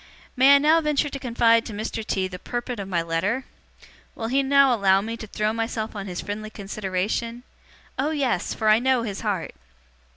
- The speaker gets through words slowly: No, average, 195 wpm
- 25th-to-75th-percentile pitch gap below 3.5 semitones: No, average, 4.2 semitones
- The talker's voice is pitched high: Yes, high, 225 Hz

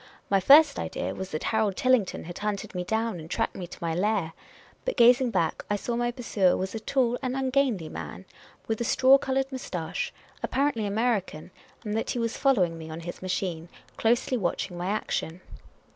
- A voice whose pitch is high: Yes, high, 215 Hz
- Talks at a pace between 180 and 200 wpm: Yes, average, 190 wpm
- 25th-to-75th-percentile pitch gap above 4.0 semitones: Yes, wide, 5.5 semitones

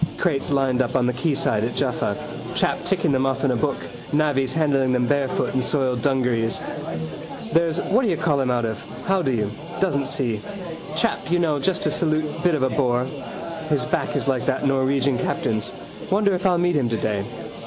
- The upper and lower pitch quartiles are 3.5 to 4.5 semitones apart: Yes, average, 4.0 semitones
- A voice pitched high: No, low, 135 Hz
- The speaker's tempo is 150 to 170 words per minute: No, average, 185 wpm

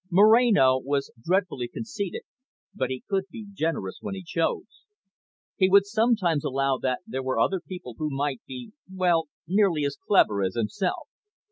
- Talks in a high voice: No, medium, 165 Hz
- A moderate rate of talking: Yes, average, 155 wpm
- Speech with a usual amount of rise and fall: No, wide, 6.7 semitones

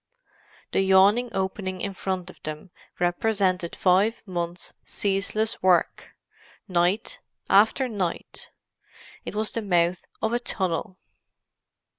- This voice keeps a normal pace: No, slow, 110 wpm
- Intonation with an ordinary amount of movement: Yes, average, 3.0 semitones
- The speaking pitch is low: No, high, 190 Hz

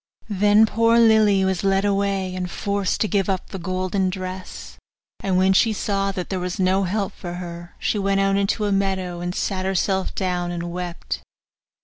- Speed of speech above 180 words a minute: Yes, average, 190 wpm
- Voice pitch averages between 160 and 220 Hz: Yes, high, 190 Hz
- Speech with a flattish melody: Yes, narrow, 1.5 semitones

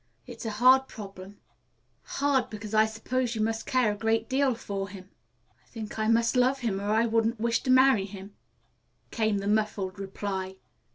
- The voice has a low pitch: No, high, 220 Hz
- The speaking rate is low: No, average, 180 wpm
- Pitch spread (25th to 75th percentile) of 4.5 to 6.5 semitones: No, average, 2.8 semitones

